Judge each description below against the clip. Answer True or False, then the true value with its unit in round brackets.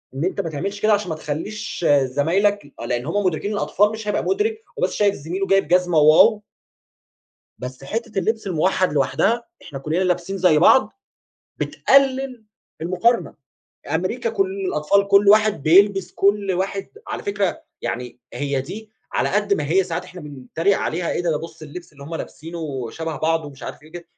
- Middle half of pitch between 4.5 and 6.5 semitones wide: True (4.8 semitones)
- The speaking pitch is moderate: True (180 Hz)